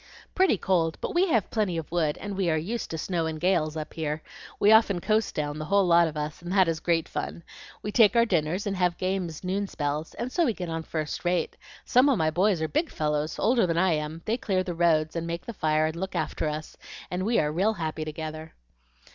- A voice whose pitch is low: No, medium, 170 Hz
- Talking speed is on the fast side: Yes, fast, 240 wpm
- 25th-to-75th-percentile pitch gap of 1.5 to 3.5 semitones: No, average, 4.1 semitones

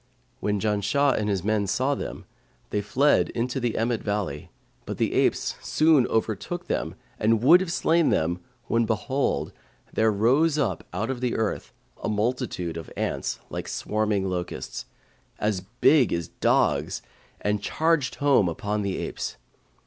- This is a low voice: Yes, low, 110 Hz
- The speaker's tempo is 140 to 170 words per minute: Yes, average, 150 wpm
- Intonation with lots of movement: No, average, 4.7 semitones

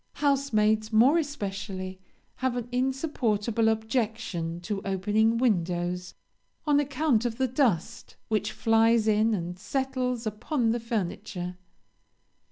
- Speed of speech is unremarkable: No, slow, 110 wpm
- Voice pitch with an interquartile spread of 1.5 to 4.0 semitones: Yes, average, 3.7 semitones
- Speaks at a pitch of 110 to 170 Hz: No, high, 225 Hz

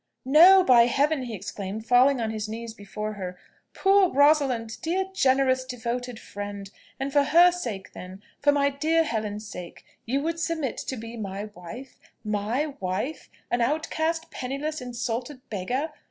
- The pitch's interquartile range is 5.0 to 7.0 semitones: Yes, wide, 5.5 semitones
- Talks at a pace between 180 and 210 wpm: No, average, 155 wpm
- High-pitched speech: Yes, very high, 250 Hz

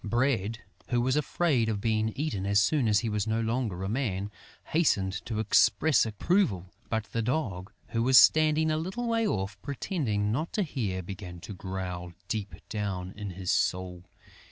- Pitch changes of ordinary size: No, wide, 5.8 semitones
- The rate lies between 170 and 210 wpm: Yes, average, 175 wpm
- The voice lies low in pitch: Yes, low, 110 Hz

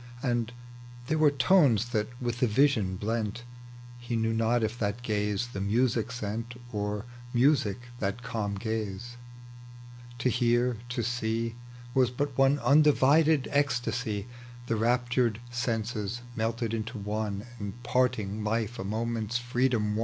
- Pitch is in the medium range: No, low, 115 Hz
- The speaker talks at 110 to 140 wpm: Yes, slow, 135 wpm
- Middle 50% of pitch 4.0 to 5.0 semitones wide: No, narrow, 2.6 semitones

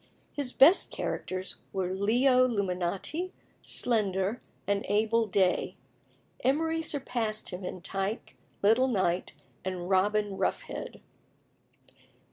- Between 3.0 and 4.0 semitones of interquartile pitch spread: No, average, 5.0 semitones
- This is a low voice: No, high, 210 Hz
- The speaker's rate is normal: No, slow, 95 wpm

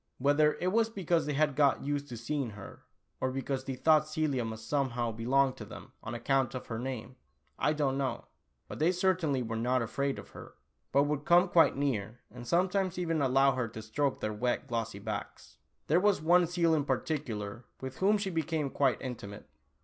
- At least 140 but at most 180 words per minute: No, average, 195 wpm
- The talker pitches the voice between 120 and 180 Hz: Yes, medium, 140 Hz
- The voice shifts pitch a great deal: No, average, 4.5 semitones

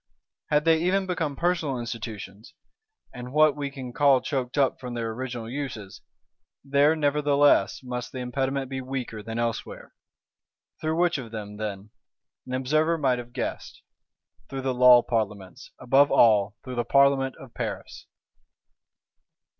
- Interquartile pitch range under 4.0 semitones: Yes, average, 3.4 semitones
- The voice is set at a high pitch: No, low, 130 Hz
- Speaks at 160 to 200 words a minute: No, average, 145 wpm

